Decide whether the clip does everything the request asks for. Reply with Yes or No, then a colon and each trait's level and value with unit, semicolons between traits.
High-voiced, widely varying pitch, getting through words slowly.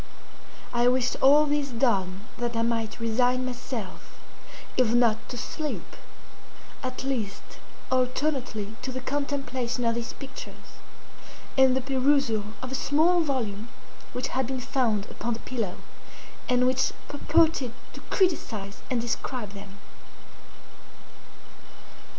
No: very high, 250 Hz; average, 2.8 semitones; slow, 120 wpm